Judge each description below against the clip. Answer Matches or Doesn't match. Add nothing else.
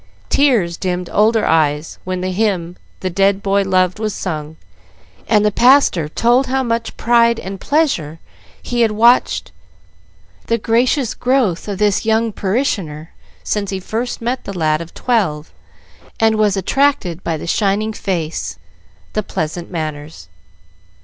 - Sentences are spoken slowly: Doesn't match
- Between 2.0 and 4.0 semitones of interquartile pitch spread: Doesn't match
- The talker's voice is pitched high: Matches